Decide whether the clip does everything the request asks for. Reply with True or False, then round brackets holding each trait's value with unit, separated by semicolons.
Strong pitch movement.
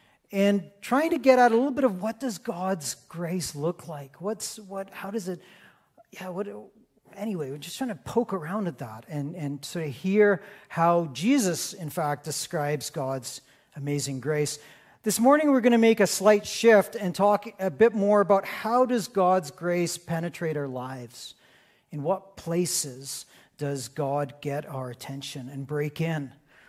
True (6.1 semitones)